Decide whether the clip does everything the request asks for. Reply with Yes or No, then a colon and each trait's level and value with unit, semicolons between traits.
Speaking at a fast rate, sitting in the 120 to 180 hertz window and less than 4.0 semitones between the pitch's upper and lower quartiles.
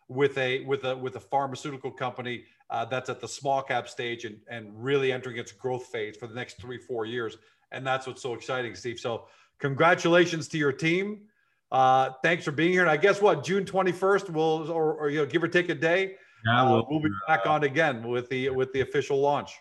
No: fast, 220 wpm; medium, 140 Hz; average, 4.3 semitones